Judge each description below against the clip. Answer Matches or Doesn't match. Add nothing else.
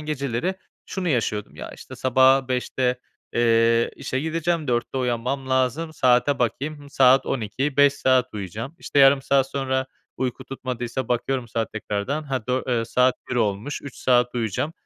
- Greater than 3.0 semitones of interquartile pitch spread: Doesn't match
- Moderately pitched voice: Doesn't match